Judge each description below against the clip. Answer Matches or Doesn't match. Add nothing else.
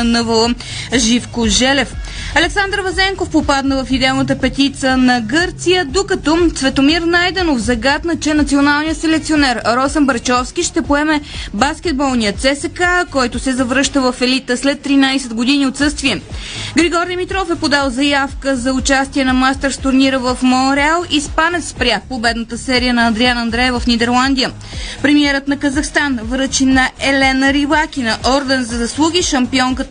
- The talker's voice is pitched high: Matches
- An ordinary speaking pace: Matches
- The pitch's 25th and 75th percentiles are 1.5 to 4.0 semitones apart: Matches